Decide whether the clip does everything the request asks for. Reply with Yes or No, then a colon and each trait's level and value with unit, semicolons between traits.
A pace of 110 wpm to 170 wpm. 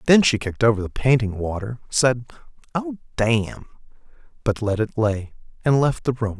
Yes: average, 150 wpm